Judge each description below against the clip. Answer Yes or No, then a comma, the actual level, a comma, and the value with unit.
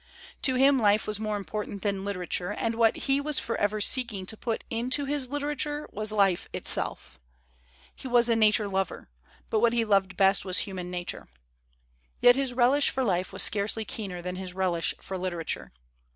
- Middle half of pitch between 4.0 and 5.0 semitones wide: Yes, average, 4.4 semitones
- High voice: Yes, high, 215 Hz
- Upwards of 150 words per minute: Yes, average, 185 wpm